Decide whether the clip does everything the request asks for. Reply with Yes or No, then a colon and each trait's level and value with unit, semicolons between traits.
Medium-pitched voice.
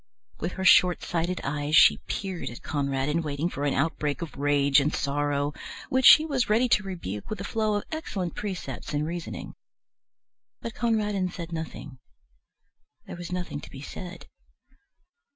Yes: medium, 170 Hz